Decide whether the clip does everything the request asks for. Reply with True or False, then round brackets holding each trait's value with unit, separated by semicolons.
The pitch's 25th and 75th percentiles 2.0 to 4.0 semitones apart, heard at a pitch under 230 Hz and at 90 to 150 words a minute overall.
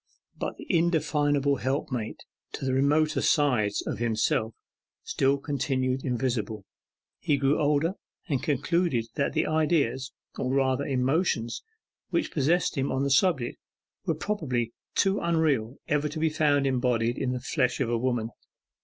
True (3.3 semitones; 135 Hz; 145 wpm)